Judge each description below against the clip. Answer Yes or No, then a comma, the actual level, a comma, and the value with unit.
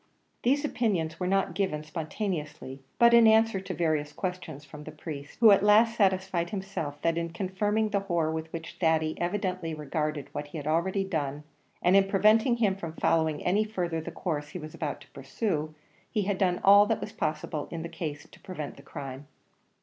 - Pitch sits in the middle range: Yes, medium, 170 Hz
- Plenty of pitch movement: No, average, 4.3 semitones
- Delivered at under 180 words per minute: No, average, 190 wpm